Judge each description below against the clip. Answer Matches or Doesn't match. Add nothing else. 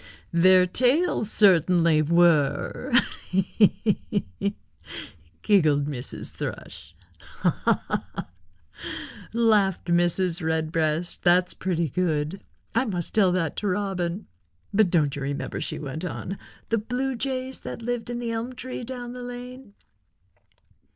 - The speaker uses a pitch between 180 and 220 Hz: Matches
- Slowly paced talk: Matches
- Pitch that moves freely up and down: Matches